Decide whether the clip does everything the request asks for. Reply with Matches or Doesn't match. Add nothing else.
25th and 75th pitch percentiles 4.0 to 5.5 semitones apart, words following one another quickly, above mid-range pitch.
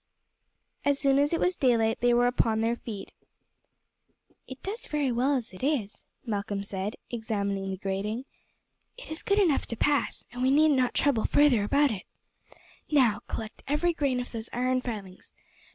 Doesn't match